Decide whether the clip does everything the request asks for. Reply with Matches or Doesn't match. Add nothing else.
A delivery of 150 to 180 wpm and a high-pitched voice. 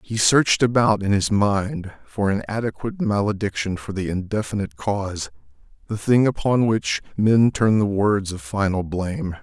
Doesn't match